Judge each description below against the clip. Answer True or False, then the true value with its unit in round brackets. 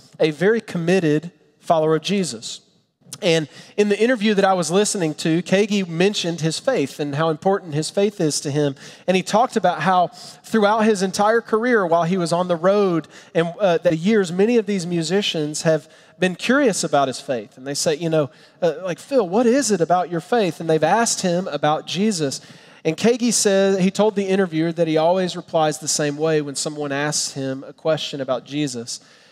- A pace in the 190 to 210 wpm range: True (200 wpm)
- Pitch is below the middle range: False (175 Hz)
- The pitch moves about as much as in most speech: True (4.4 semitones)